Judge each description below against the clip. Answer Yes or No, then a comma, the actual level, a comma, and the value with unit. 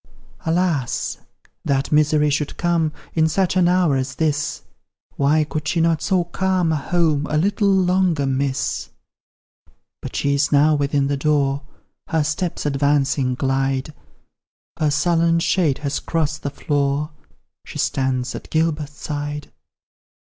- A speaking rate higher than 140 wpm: No, slow, 135 wpm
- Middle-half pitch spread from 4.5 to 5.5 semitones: No, average, 2.8 semitones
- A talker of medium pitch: Yes, medium, 150 Hz